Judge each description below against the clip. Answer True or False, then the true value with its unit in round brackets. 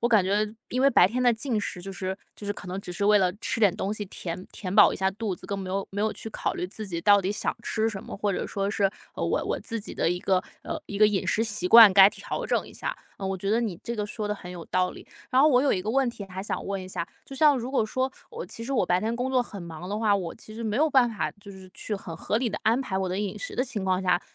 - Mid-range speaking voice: False (205 Hz)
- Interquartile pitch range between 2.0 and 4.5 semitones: True (3.3 semitones)